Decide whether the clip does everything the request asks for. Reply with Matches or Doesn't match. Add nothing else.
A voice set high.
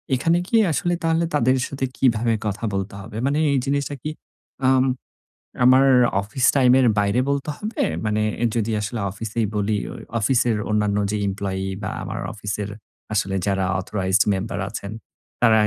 Doesn't match